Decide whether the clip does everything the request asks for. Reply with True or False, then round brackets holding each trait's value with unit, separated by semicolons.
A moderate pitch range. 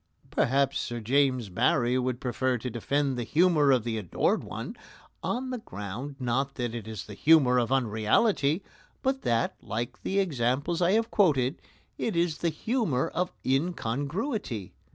False (6.1 semitones)